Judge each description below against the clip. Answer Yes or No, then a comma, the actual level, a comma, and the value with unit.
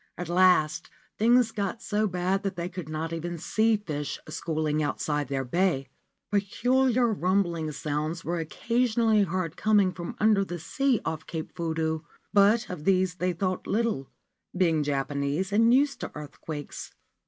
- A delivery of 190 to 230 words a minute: No, average, 150 wpm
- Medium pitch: Yes, medium, 180 Hz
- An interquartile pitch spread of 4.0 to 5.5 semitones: Yes, average, 4.9 semitones